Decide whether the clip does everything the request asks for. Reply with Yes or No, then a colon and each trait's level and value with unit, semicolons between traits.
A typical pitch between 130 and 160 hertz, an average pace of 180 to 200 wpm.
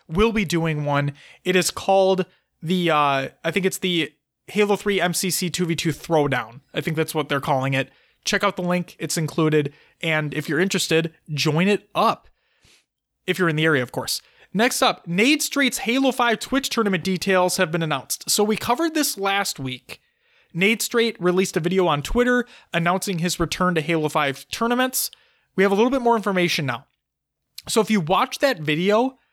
No: medium, 180 Hz; average, 185 wpm